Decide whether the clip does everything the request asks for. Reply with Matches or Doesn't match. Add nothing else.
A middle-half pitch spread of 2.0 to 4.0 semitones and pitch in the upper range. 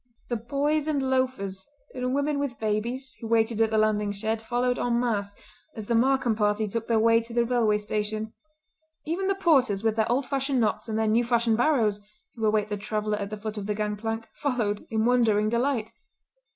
Matches